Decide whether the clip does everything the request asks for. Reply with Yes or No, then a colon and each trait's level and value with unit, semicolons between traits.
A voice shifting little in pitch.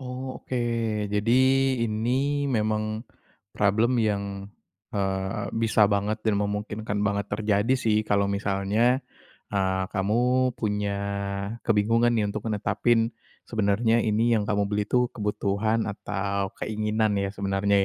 Yes: narrow, 2.2 semitones